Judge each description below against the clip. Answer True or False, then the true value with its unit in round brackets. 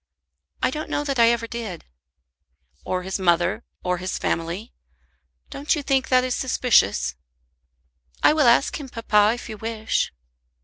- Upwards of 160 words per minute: False (150 wpm)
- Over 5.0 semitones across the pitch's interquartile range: True (5.6 semitones)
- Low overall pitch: False (230 Hz)